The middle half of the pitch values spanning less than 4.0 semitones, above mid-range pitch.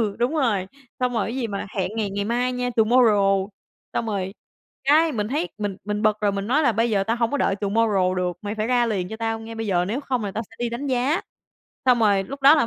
Yes: average, 3.5 semitones; high, 225 Hz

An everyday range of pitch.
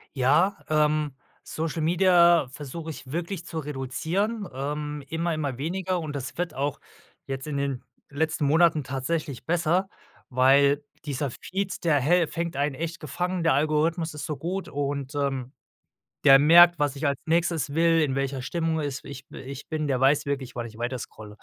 Yes: average, 3.3 semitones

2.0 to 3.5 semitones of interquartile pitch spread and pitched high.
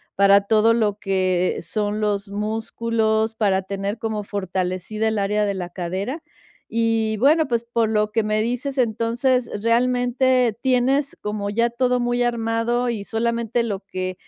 Yes: average, 2.8 semitones; high, 220 Hz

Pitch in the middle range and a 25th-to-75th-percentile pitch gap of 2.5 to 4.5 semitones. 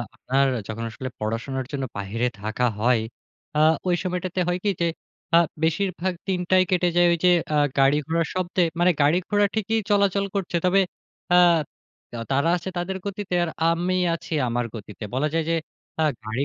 No: medium, 170 Hz; wide, 5.6 semitones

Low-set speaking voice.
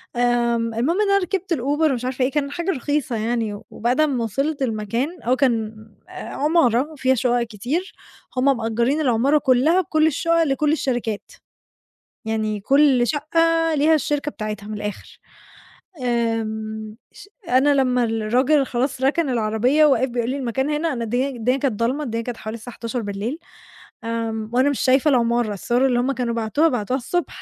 No: very high, 250 Hz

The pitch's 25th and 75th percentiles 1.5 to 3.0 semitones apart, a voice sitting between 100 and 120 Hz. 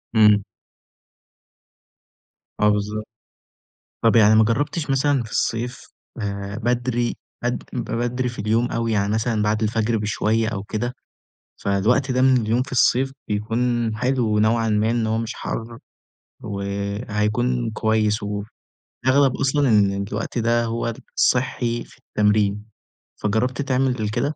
Yes: narrow, 2.6 semitones; low, 115 Hz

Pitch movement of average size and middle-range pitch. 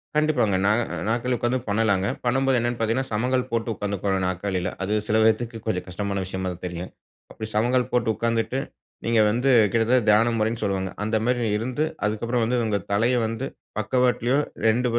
No: average, 3.2 semitones; low, 115 Hz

